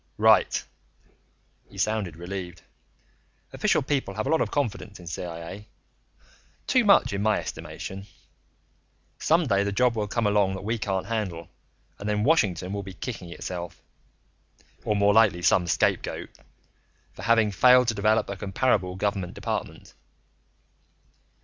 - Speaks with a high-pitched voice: No, low, 100 Hz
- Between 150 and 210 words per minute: No, average, 140 wpm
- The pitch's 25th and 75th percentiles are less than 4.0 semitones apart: Yes, average, 3.3 semitones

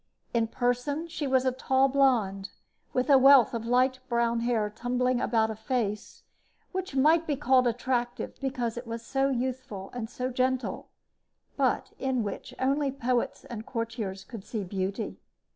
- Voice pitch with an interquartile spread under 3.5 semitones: Yes, narrow, 2.5 semitones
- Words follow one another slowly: No, average, 160 wpm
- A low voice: No, high, 245 Hz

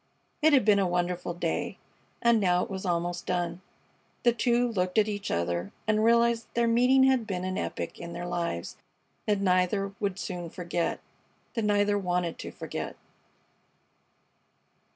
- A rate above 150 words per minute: Yes, average, 160 wpm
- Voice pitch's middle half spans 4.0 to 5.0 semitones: Yes, average, 4.3 semitones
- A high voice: Yes, high, 195 Hz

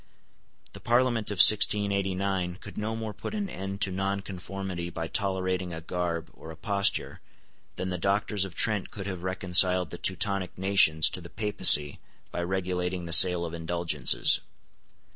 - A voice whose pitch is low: Yes, very low, 95 Hz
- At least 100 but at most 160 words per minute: Yes, average, 155 wpm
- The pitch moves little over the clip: Yes, narrow, 2.1 semitones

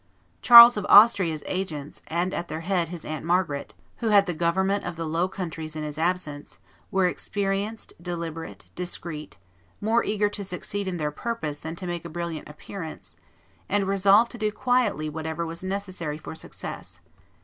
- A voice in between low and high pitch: Yes, medium, 175 Hz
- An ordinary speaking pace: Yes, average, 170 wpm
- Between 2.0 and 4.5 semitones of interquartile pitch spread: Yes, average, 3.8 semitones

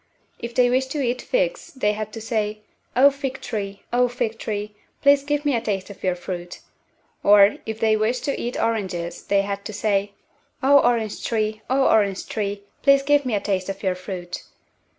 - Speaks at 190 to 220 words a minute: Yes, average, 195 wpm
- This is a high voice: Yes, high, 215 Hz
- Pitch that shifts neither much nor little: Yes, average, 4.1 semitones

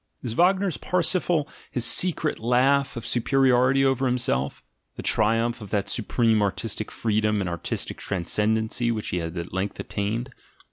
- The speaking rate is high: No, average, 145 wpm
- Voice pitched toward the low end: Yes, low, 115 Hz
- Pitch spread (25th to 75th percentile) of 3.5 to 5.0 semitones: Yes, average, 4.2 semitones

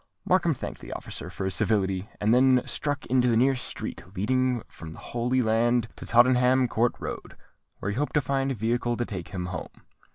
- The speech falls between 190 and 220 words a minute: Yes, average, 200 wpm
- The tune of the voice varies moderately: Yes, average, 3.2 semitones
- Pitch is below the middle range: Yes, low, 120 Hz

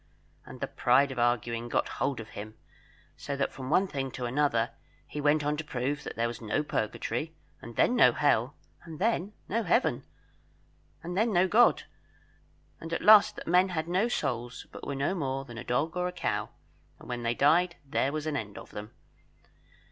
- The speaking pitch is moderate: Yes, medium, 145 Hz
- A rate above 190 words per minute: Yes, average, 200 wpm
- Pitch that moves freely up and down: Yes, wide, 6.5 semitones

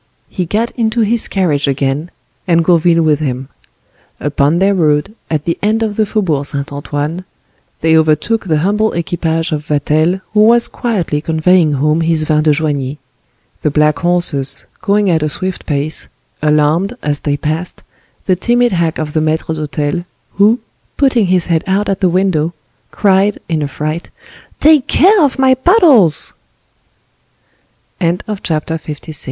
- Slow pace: No, average, 160 wpm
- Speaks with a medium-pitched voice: Yes, medium, 165 Hz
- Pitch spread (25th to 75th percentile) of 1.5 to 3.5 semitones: No, average, 4.7 semitones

